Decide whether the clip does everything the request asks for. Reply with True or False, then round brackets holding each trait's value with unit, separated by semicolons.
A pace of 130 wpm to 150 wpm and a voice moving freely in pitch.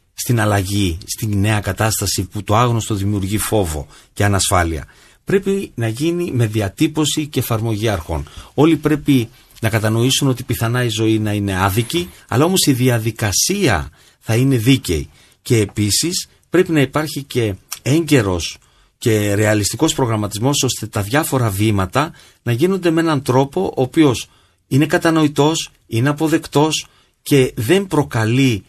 True (140 wpm; 6.0 semitones)